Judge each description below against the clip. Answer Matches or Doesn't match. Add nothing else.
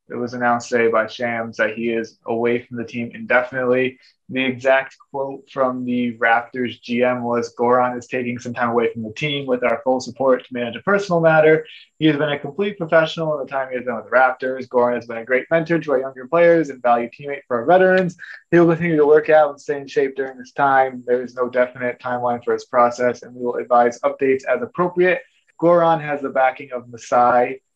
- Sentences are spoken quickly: Matches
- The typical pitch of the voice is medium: Doesn't match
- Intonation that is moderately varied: Matches